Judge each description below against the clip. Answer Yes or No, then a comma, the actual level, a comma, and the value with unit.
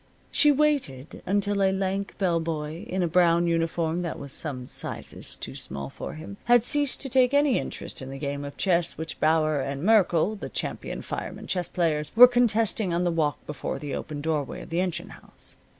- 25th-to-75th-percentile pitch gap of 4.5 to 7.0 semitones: Yes, average, 4.8 semitones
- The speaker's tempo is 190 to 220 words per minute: Yes, average, 200 wpm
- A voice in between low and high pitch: Yes, medium, 170 Hz